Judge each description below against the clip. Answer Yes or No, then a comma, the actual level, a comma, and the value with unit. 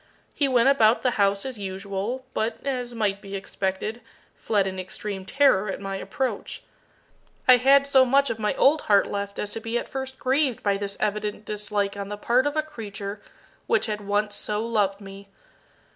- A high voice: Yes, high, 210 Hz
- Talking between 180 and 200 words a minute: Yes, average, 190 wpm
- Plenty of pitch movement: No, average, 4.3 semitones